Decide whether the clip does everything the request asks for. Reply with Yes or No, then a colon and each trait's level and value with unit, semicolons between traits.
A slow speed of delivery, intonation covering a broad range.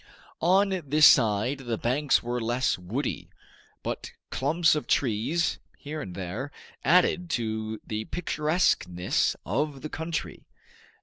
Yes: slow, 120 wpm; wide, 6.1 semitones